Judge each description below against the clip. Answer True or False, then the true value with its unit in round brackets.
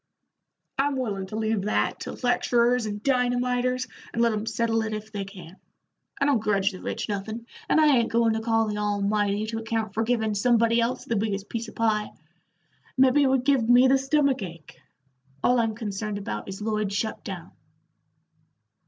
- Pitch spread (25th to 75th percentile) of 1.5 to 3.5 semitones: True (2.9 semitones)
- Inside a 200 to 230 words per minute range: False (185 wpm)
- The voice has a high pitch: True (225 Hz)